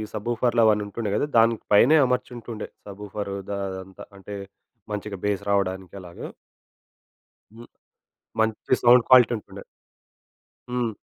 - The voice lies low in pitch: Yes, low, 105 Hz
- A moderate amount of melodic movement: Yes, average, 3.0 semitones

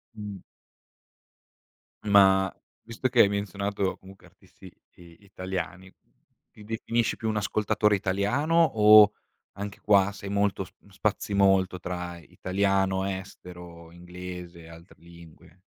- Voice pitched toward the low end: Yes, very low, 95 Hz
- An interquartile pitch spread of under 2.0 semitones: No, narrow, 2.3 semitones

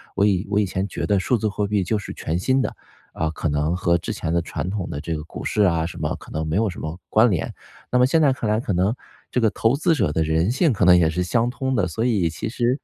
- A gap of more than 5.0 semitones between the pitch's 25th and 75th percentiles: Yes, wide, 5.4 semitones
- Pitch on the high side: No, low, 100 Hz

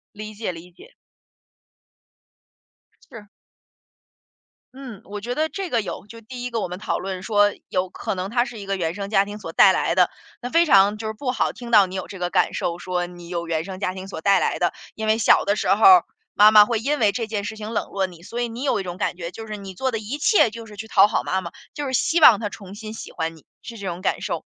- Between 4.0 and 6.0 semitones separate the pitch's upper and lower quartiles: No, average, 3.6 semitones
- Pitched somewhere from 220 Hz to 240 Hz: No, high, 210 Hz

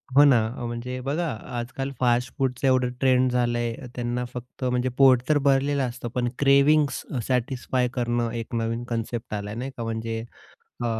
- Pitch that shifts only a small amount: Yes, narrow, 2.1 semitones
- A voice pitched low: Yes, low, 125 Hz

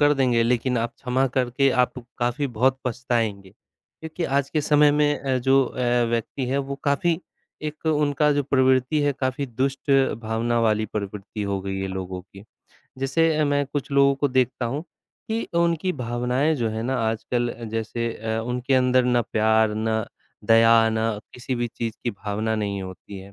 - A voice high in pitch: No, low, 125 Hz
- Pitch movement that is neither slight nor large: Yes, average, 3.9 semitones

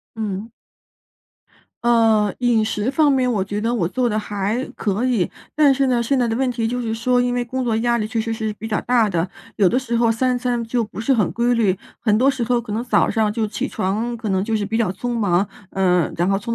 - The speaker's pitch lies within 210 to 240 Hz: Yes, high, 225 Hz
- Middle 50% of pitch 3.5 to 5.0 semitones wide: No, average, 2.7 semitones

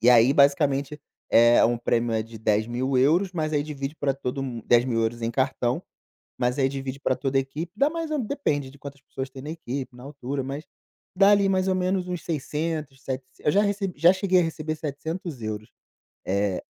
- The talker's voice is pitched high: No, medium, 140 Hz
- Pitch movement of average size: Yes, average, 4.7 semitones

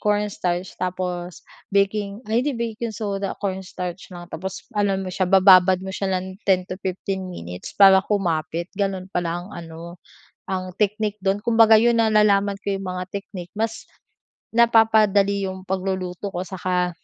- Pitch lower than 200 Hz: Yes, high, 190 Hz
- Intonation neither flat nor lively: No, narrow, 2.2 semitones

